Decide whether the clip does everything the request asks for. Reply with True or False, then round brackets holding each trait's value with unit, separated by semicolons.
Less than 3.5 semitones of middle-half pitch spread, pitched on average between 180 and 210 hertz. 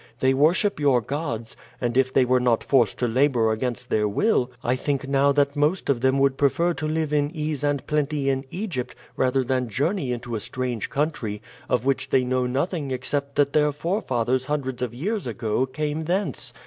False (3.0 semitones; 135 Hz)